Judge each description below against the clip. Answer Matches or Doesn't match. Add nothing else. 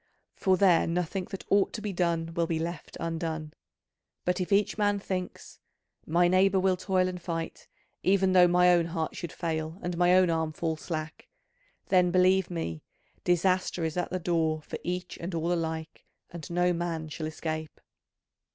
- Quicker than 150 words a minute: Matches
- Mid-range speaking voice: Matches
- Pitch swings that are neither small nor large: Doesn't match